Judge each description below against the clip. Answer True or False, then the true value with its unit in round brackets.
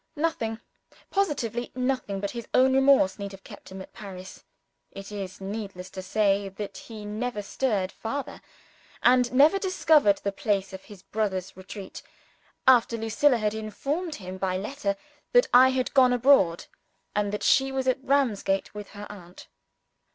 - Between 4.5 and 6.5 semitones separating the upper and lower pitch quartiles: True (4.9 semitones)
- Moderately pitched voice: False (215 Hz)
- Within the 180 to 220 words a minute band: False (160 wpm)